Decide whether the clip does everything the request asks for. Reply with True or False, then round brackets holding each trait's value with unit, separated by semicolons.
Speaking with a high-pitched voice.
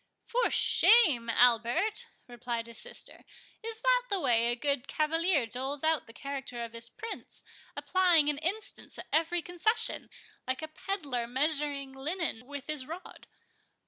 True (290 Hz)